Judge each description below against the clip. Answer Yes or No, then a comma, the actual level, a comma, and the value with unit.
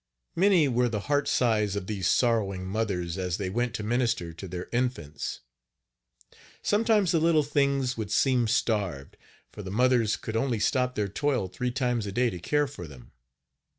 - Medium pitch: No, low, 115 Hz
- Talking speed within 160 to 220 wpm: Yes, average, 175 wpm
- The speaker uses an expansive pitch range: No, average, 5.0 semitones